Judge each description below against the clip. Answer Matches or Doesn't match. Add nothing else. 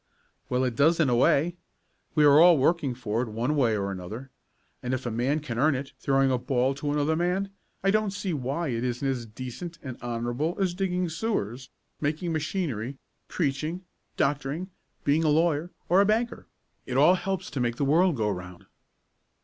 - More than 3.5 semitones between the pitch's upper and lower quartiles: Matches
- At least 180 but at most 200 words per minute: Matches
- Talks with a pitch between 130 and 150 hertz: Matches